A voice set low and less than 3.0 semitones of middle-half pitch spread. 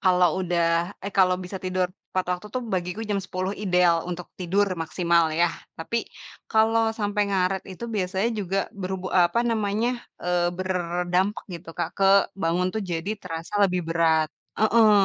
No: medium, 185 Hz; narrow, 2.4 semitones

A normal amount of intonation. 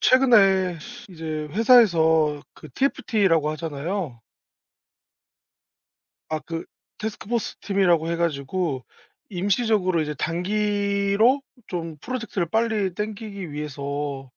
Yes: average, 5.0 semitones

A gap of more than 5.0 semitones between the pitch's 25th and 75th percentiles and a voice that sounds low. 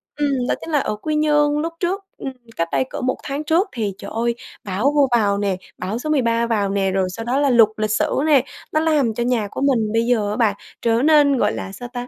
No: wide, 5.4 semitones; high, 245 Hz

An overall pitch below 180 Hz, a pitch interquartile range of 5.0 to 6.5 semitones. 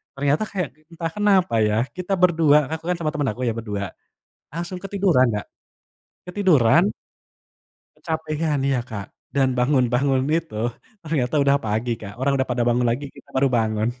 Yes: medium, 140 Hz; average, 5.3 semitones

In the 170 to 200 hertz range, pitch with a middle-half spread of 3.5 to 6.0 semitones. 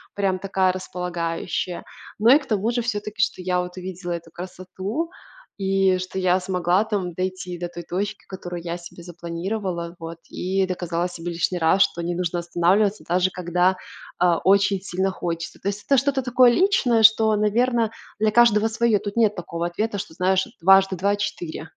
No: medium, 185 Hz; average, 3.1 semitones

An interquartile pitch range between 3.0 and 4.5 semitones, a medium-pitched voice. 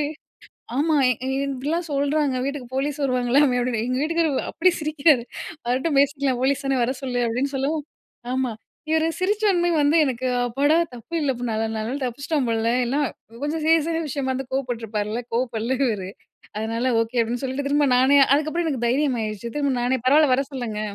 No: average, 3.3 semitones; very high, 270 Hz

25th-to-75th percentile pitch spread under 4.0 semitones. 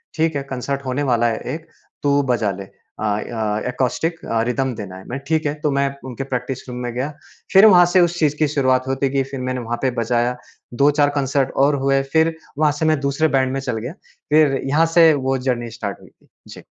Yes: average, 3.3 semitones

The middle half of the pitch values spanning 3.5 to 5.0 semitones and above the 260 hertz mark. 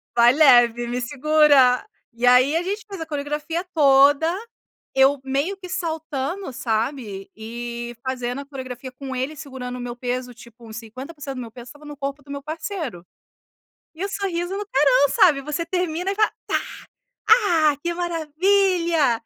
Yes: average, 4.7 semitones; very high, 280 Hz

